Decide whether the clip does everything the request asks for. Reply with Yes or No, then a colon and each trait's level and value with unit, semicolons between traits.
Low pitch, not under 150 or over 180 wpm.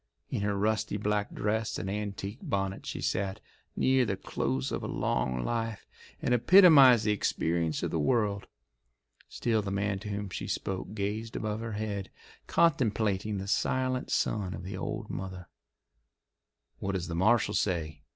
Yes: low, 105 Hz; average, 160 wpm